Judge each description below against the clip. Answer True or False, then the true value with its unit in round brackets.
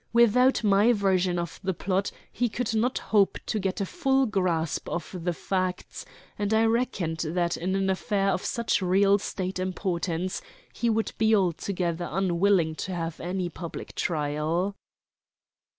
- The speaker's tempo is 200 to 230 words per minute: False (150 wpm)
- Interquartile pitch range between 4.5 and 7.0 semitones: False (3.2 semitones)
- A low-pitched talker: False (190 Hz)